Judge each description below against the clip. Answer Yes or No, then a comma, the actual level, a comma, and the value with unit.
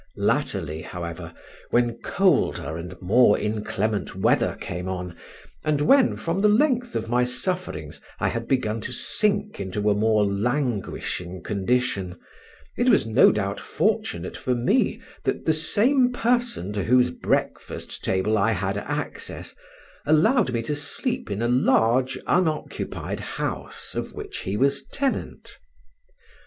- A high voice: No, low, 120 Hz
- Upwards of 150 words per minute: No, slow, 135 wpm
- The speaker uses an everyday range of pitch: No, wide, 7.7 semitones